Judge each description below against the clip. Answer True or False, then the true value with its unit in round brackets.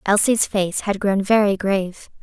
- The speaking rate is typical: True (160 wpm)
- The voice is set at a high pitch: True (200 Hz)